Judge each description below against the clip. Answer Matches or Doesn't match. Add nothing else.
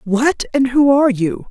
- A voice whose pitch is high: Matches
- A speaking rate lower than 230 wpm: Matches